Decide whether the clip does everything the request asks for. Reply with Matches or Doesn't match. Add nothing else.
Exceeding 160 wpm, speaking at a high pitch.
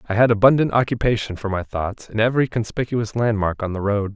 Doesn't match